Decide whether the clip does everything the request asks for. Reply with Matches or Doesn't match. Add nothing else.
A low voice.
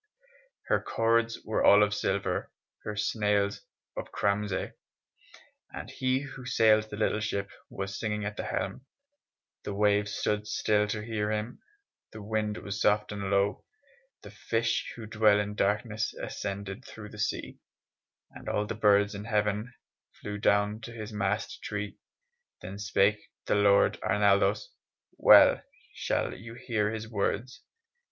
Matches